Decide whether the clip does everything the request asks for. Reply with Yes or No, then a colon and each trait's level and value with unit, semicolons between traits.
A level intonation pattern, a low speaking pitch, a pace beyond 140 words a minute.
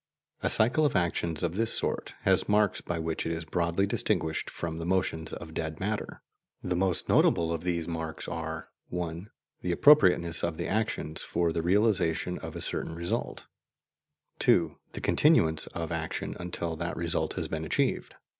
Yes: narrow, 2.2 semitones; very low, 85 Hz; average, 170 wpm